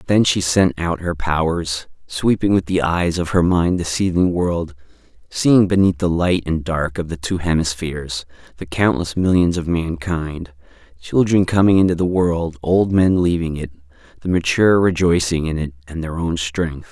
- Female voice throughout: No, male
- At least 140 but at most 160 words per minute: No, average, 170 wpm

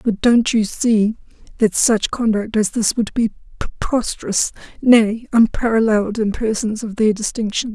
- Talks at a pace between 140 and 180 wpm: Yes, average, 145 wpm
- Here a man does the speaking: No, female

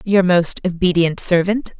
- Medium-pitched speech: Yes, medium, 180 Hz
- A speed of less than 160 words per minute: Yes, slow, 135 wpm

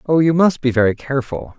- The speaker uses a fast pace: Yes, fast, 225 wpm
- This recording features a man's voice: Yes, male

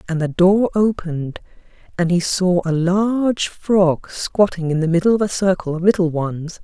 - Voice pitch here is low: No, medium, 180 Hz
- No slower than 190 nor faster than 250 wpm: No, average, 180 wpm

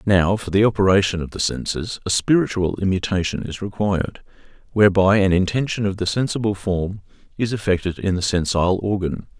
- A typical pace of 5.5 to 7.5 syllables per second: Yes, 5.7 syllables/s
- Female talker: No, male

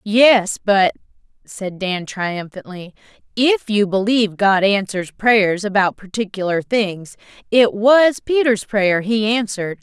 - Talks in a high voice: Yes, high, 210 Hz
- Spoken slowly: Yes, slow, 120 wpm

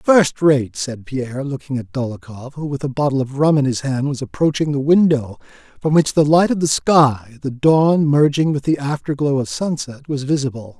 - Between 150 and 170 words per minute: No, fast, 205 wpm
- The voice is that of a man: Yes, male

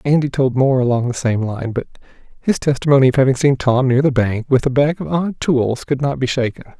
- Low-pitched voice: Yes, low, 130 Hz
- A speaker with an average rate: No, fast, 240 wpm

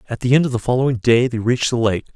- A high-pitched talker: No, low, 120 Hz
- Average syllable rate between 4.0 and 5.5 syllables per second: No, 7.5 syllables/s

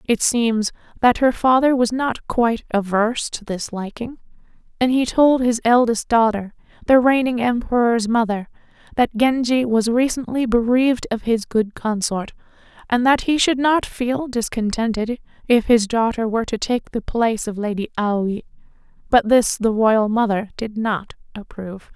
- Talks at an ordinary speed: Yes, average, 155 wpm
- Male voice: No, female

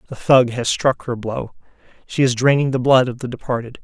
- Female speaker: No, male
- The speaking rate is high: Yes, fast, 220 wpm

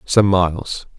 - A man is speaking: Yes, male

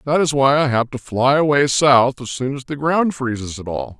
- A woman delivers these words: No, male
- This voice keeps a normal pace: No, fast, 255 wpm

